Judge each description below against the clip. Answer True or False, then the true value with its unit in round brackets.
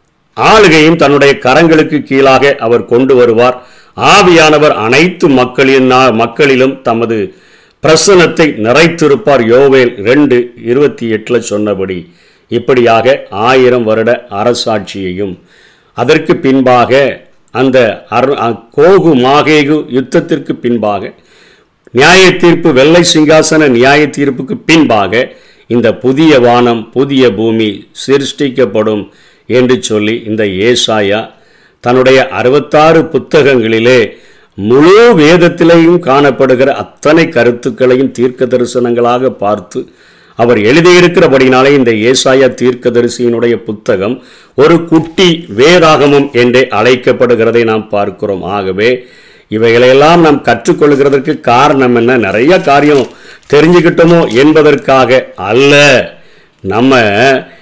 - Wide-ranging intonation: False (4.3 semitones)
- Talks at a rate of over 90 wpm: False (85 wpm)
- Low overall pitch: True (130 Hz)